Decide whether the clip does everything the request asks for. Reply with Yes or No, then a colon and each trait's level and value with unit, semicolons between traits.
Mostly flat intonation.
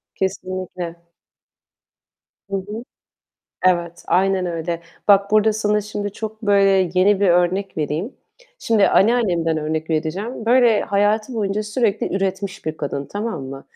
No: average, 3.5 semitones